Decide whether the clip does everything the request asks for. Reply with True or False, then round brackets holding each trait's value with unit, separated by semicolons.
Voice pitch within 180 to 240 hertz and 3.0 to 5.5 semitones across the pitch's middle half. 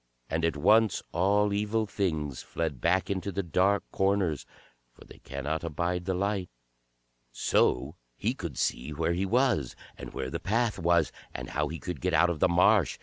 False (90 Hz; 4.0 semitones)